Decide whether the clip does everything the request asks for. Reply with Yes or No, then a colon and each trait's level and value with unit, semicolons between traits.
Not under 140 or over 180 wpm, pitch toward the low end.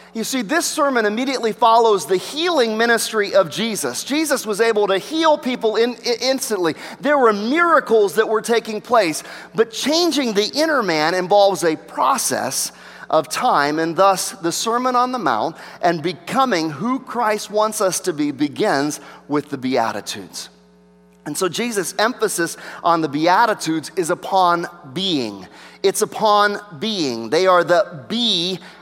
No: average, 150 wpm; high, 210 Hz